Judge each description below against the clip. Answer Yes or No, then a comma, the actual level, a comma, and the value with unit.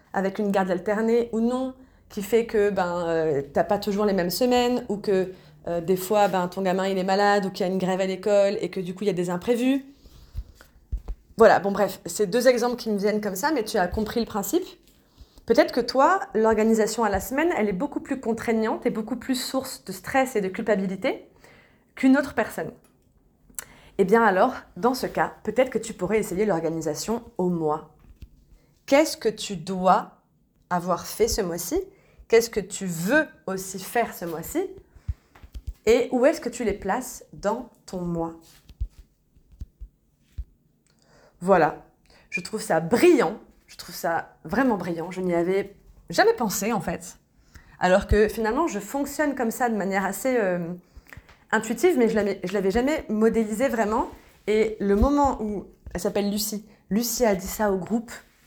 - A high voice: Yes, high, 210 Hz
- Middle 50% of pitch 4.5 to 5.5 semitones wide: No, average, 4.1 semitones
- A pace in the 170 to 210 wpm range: Yes, average, 180 wpm